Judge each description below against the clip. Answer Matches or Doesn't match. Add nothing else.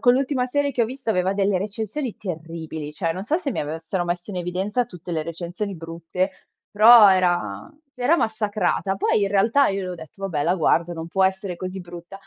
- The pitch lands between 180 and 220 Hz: Matches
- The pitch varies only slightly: Doesn't match